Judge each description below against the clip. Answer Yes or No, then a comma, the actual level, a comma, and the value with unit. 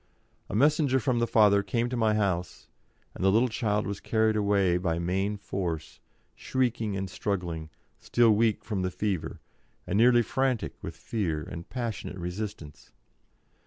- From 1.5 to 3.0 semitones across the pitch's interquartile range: No, average, 3.9 semitones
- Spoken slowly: No, average, 155 wpm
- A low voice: Yes, low, 105 Hz